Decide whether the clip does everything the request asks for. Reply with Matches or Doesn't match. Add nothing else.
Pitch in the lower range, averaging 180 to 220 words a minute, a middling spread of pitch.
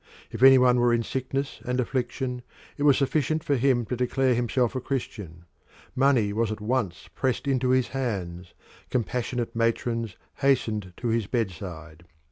Doesn't match